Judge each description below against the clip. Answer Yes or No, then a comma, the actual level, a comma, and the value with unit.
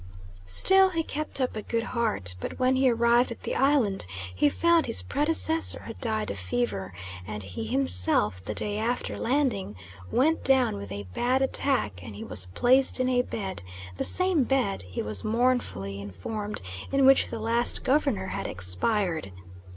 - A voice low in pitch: No, high, 225 Hz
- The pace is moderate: Yes, average, 170 wpm